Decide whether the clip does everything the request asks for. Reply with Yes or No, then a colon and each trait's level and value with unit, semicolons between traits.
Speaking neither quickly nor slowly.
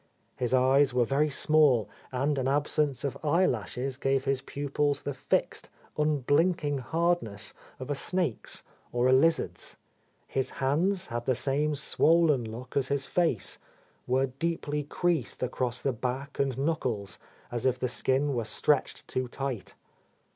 Yes: average, 155 wpm